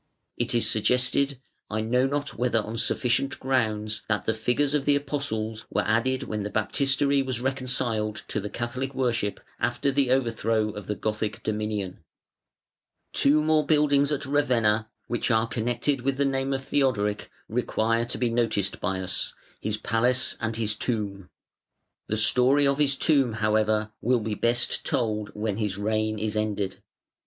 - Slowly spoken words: No, average, 160 wpm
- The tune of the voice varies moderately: Yes, average, 3.7 semitones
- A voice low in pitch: Yes, low, 115 Hz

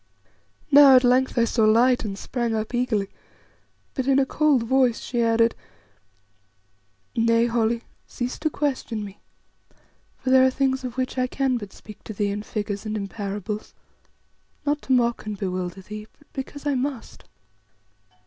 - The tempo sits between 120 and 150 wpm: No, average, 165 wpm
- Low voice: No, high, 235 Hz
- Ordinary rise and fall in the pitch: Yes, average, 3.6 semitones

